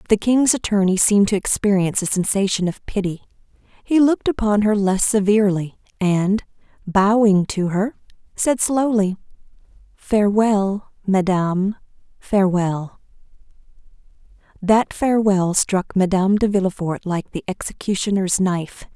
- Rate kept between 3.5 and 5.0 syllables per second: Yes, 4.8 syllables/s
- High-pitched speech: Yes, high, 200 Hz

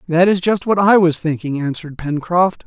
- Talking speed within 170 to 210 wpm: Yes, average, 200 wpm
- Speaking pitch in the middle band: Yes, medium, 170 Hz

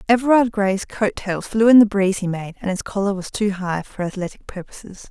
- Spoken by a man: No, female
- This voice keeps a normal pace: No, fast, 225 wpm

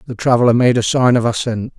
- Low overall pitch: Yes, low, 120 Hz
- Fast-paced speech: Yes, fast, 235 wpm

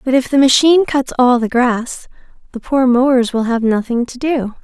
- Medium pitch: No, very high, 255 Hz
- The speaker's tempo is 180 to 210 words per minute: Yes, fast, 205 wpm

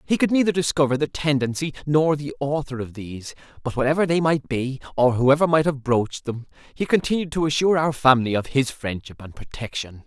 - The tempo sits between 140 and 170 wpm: No, average, 195 wpm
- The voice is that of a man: Yes, male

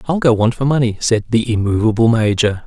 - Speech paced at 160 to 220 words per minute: Yes, fast, 205 wpm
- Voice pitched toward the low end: Yes, low, 115 Hz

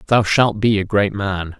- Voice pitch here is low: Yes, low, 100 Hz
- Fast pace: Yes, fast, 225 wpm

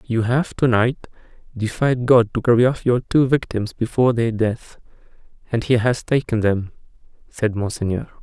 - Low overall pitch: Yes, low, 115 Hz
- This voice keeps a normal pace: Yes, average, 160 wpm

